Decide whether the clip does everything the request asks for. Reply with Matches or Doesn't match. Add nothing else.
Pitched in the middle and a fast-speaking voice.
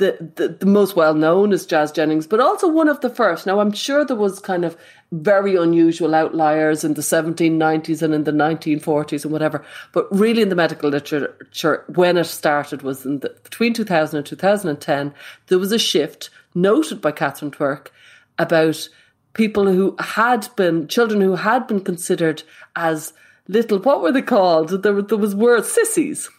Doesn't match